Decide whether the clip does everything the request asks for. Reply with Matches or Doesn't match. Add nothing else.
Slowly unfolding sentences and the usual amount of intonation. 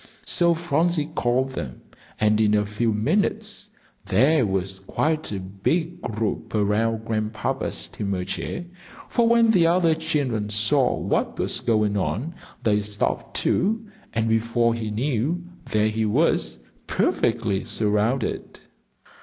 Doesn't match